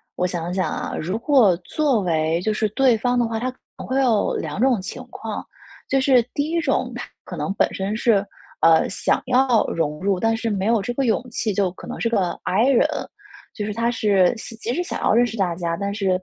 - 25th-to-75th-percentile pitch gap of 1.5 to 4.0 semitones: No, average, 4.6 semitones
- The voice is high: Yes, high, 215 Hz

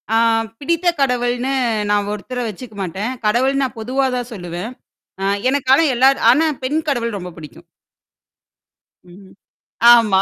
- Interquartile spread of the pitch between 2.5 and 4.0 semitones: No, average, 4.5 semitones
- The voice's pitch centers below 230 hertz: No, high, 240 Hz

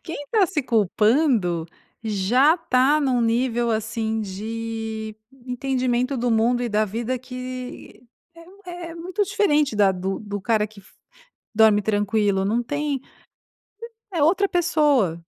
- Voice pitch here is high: Yes, high, 240 Hz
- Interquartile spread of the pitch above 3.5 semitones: Yes, average, 5.1 semitones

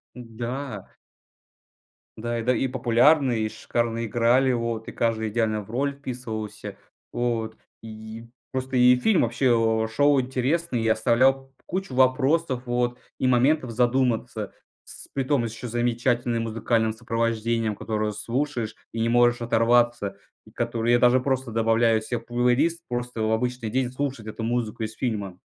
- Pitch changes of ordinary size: No, narrow, 2.2 semitones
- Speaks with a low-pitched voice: Yes, low, 120 Hz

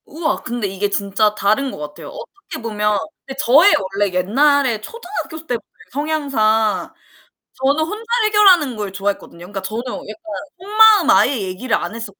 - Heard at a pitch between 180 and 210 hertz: No, high, 245 Hz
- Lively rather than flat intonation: Yes, wide, 7.5 semitones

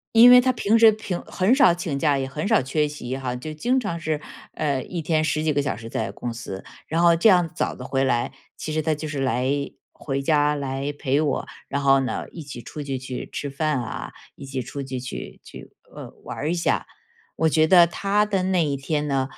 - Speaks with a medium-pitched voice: Yes, medium, 150 Hz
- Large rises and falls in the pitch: No, average, 4.0 semitones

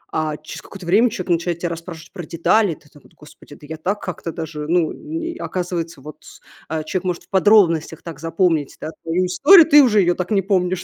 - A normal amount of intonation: Yes, average, 3.2 semitones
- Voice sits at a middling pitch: Yes, medium, 175 Hz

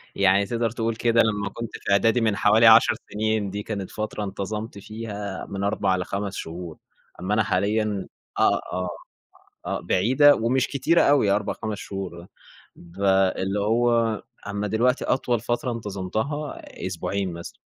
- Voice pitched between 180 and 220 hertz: No, low, 105 Hz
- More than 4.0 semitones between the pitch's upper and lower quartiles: No, average, 2.7 semitones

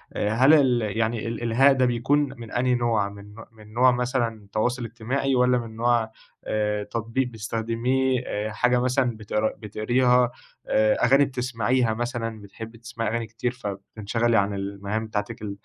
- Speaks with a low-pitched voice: Yes, low, 115 Hz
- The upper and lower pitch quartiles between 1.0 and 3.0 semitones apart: Yes, narrow, 2.5 semitones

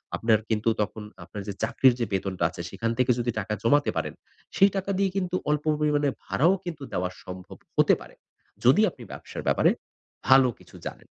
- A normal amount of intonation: No, wide, 6.4 semitones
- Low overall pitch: Yes, low, 125 Hz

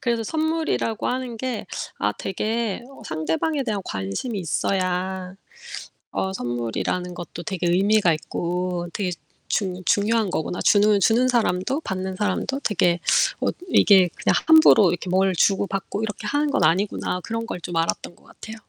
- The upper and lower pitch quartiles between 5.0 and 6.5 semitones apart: No, average, 4.2 semitones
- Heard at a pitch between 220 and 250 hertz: No, high, 195 Hz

